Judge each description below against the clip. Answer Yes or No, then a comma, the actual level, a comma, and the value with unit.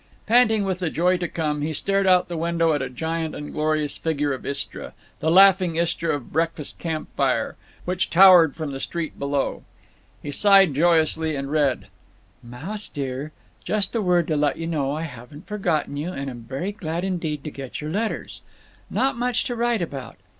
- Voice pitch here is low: No, medium, 160 Hz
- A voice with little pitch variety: No, average, 4.0 semitones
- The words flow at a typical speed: Yes, average, 185 wpm